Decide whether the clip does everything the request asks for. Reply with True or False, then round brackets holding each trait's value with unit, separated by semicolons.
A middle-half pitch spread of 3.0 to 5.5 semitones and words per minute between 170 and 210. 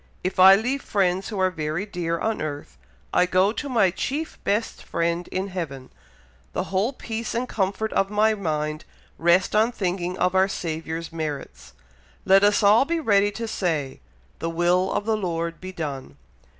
True (4.0 semitones; 175 wpm)